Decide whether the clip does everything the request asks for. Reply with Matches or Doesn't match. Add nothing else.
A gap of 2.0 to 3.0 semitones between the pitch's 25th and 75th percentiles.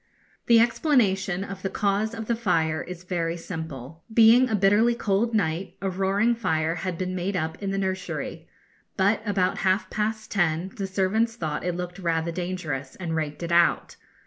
Doesn't match